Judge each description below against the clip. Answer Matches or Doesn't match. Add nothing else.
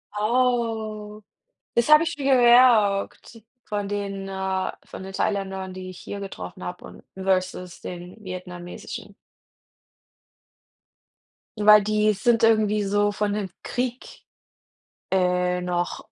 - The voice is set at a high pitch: Matches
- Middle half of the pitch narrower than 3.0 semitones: Matches